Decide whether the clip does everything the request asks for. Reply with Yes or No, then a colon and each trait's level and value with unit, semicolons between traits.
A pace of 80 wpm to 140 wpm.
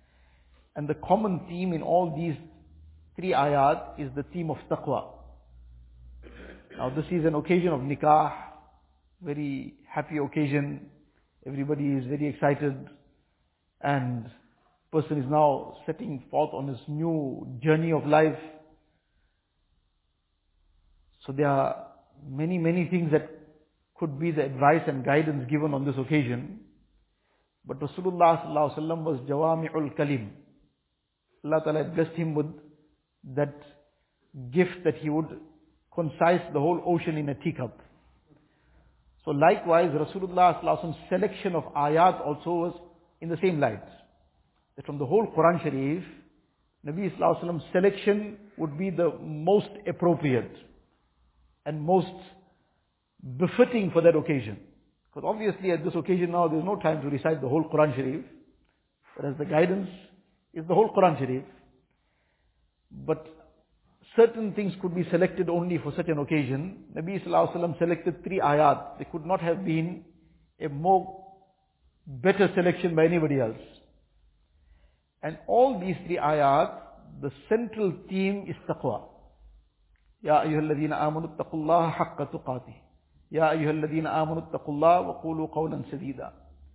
Yes: slow, 135 wpm